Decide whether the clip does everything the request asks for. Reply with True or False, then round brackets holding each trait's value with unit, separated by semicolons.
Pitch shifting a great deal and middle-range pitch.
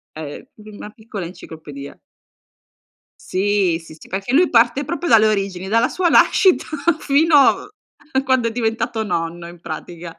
False (6.9 semitones; 215 Hz)